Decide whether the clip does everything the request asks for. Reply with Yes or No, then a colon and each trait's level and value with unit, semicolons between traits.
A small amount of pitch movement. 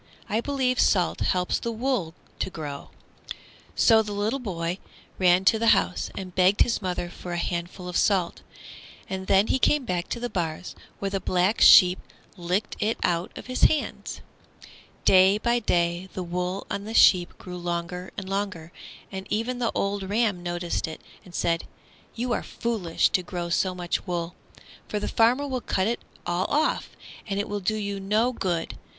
No: average, 3.8 semitones